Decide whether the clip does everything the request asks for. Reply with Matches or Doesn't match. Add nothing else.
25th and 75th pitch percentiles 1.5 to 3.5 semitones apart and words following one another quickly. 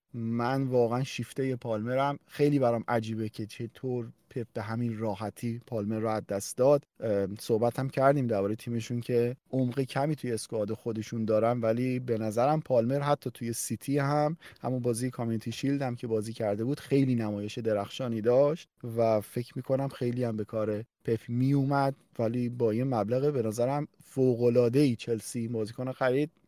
Matches